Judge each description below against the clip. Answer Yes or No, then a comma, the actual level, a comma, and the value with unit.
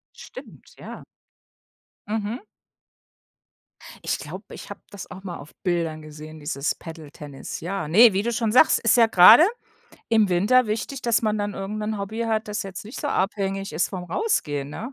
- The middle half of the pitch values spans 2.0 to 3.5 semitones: No, average, 4.8 semitones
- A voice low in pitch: No, high, 200 Hz